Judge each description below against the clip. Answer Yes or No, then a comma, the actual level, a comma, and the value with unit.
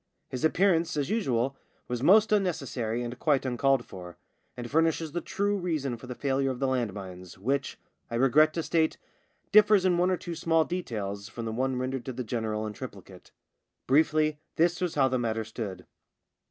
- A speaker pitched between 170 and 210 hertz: No, low, 135 Hz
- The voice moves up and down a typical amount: No, wide, 5.7 semitones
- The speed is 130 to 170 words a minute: No, average, 190 wpm